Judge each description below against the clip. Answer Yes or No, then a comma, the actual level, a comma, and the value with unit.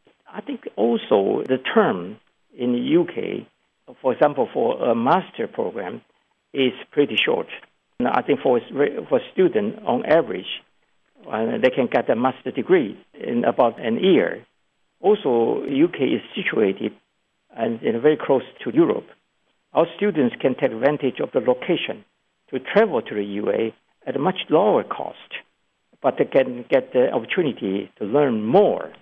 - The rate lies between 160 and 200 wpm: No, average, 145 wpm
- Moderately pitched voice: Yes, medium, 145 Hz